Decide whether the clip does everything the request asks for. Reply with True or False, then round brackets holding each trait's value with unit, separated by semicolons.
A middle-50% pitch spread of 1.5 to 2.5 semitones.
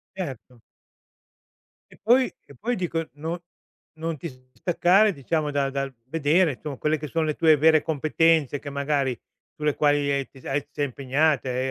False (2.9 semitones)